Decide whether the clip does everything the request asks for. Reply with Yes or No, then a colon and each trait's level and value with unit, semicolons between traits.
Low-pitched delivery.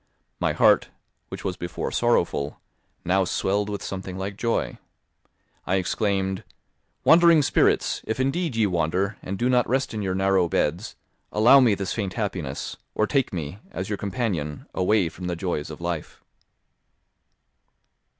Yes: very low, 95 Hz